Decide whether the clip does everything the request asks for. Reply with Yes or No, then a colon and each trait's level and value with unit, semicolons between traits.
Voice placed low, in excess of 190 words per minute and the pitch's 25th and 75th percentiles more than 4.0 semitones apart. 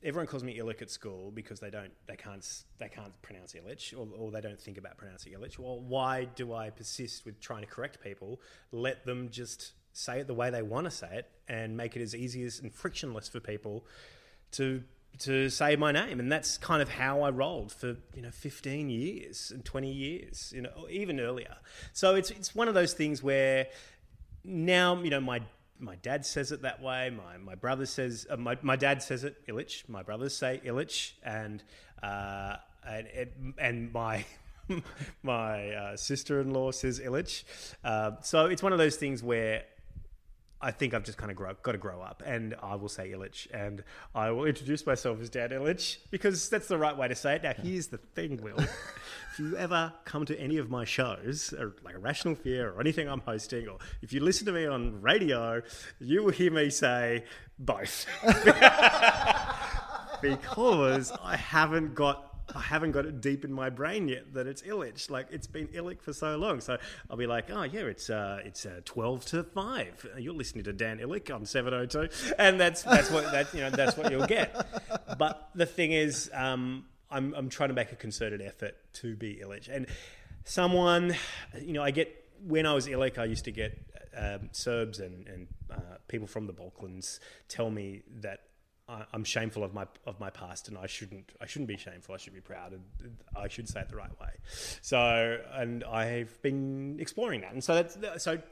Yes: low, 125 Hz; fast, 205 wpm; average, 5.0 semitones